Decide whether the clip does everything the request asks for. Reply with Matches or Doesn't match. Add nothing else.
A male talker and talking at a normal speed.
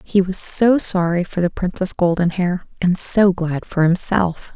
Doesn't match